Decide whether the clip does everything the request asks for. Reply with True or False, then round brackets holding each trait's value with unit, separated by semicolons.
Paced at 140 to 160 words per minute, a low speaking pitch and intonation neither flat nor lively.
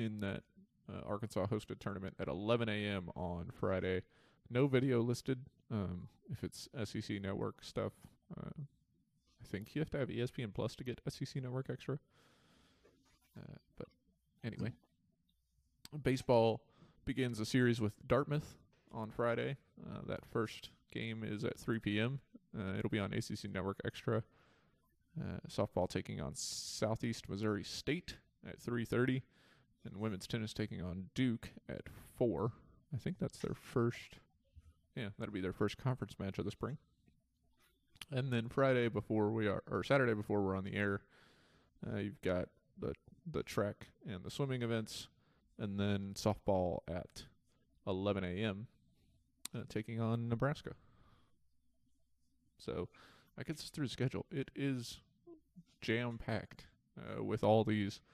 True (145 wpm; 110 Hz; 4.1 semitones)